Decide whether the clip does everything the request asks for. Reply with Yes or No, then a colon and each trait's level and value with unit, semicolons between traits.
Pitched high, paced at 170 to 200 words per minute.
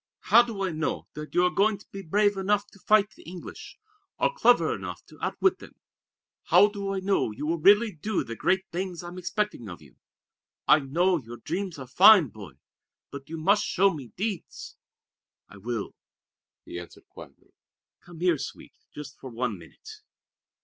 No: medium, 180 Hz; average, 180 wpm